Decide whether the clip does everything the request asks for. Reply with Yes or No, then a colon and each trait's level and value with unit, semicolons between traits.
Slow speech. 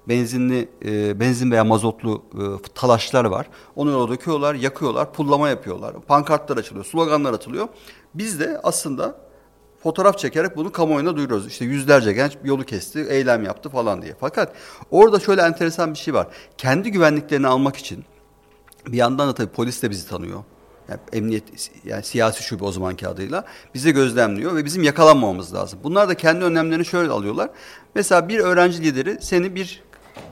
No: fast, 160 wpm